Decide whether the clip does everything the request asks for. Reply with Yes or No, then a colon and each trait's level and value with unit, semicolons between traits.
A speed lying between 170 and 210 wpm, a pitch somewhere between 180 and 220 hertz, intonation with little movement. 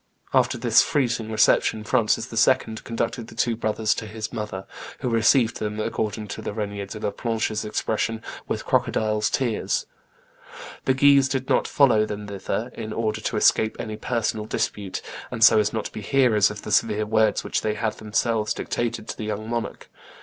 No: average, 180 wpm; low, 110 Hz; narrow, 1.4 semitones